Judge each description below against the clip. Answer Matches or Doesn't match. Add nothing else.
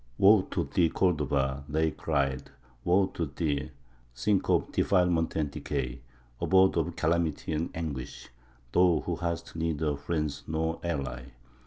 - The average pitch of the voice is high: Doesn't match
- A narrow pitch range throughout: Doesn't match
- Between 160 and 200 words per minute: Doesn't match